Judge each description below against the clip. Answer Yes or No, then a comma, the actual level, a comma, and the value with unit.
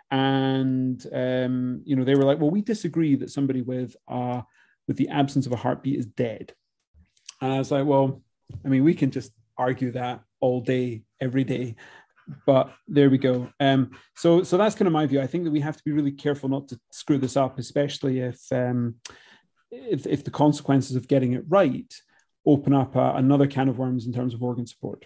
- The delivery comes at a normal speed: No, fast, 210 wpm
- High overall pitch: No, low, 135 Hz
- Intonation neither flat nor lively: No, narrow, 2.0 semitones